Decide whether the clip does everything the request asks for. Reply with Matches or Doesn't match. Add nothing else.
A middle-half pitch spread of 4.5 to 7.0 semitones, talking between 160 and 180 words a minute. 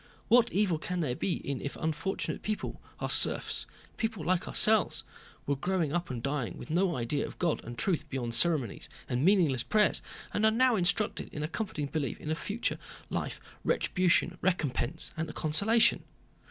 Matches